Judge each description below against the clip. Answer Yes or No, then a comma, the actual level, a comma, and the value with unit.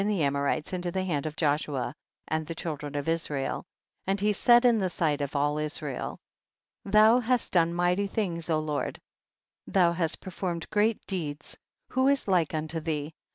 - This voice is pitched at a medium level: Yes, medium, 165 Hz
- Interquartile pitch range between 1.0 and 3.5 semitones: No, average, 4.5 semitones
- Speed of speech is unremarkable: Yes, average, 180 wpm